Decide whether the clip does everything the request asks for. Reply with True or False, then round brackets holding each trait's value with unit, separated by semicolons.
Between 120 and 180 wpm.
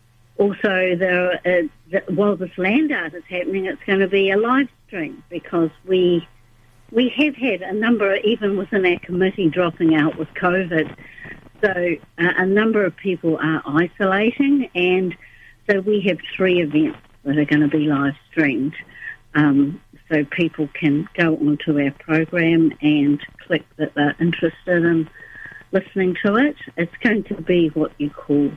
True (165 wpm)